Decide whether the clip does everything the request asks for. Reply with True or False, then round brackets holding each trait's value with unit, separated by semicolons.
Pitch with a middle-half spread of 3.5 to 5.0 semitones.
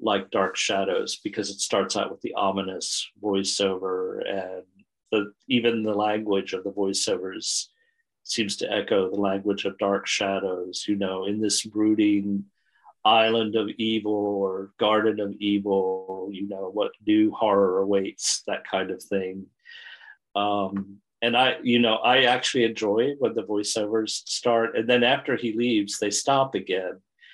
False (2.7 semitones)